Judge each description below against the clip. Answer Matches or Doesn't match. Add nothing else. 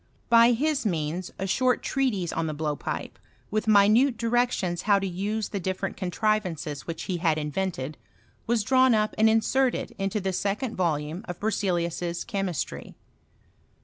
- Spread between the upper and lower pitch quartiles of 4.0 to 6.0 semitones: Matches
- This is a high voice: Matches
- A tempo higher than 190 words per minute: Doesn't match